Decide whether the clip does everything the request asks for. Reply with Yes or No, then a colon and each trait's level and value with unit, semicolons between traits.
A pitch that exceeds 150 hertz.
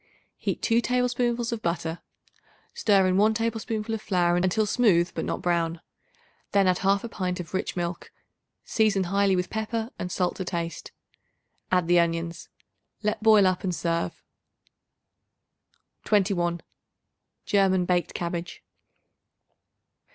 Yes: medium, 185 Hz